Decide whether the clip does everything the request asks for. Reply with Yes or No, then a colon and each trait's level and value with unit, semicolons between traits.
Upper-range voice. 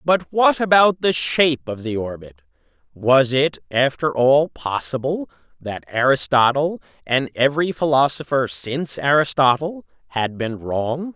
No: medium, 140 Hz